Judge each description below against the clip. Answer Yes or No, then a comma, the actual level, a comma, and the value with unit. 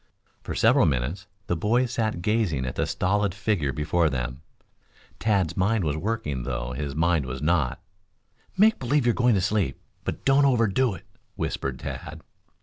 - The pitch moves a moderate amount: No, wide, 7.7 semitones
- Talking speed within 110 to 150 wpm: No, average, 160 wpm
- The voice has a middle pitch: No, very low, 90 Hz